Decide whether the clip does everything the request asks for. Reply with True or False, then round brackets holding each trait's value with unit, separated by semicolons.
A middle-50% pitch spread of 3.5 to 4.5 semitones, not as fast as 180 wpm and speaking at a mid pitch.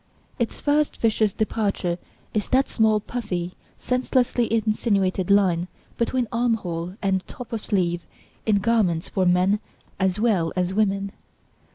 False (3.8 semitones; 135 wpm; 205 Hz)